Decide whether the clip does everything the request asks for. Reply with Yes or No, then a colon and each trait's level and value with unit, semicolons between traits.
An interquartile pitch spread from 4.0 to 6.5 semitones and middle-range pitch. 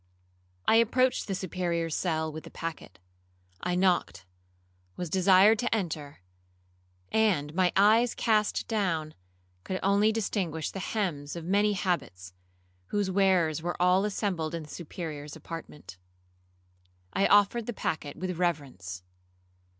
Yes: average, 4.3 semitones; medium, 180 Hz